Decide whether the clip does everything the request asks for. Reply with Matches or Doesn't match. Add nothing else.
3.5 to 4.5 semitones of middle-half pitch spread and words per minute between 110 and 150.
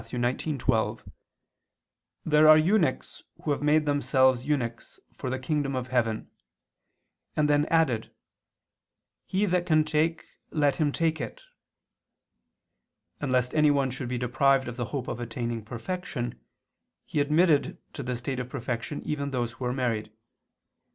Matches